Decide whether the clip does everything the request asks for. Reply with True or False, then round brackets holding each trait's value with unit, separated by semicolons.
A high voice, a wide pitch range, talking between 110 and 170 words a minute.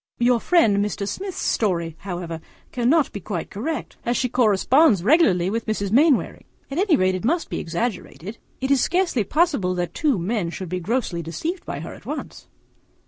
False (225 Hz; 7.4 semitones; 185 wpm)